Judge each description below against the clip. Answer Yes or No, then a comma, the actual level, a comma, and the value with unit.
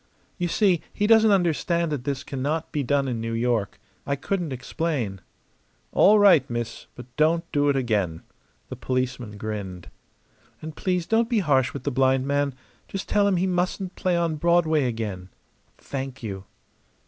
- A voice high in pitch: No, medium, 140 Hz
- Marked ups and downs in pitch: Yes, wide, 6.0 semitones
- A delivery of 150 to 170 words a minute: Yes, average, 165 wpm